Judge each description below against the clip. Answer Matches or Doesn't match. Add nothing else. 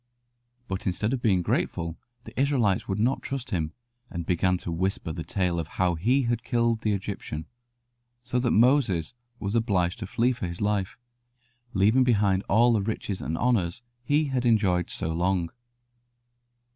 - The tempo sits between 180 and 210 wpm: Doesn't match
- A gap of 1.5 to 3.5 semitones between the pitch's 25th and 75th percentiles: Doesn't match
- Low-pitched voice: Matches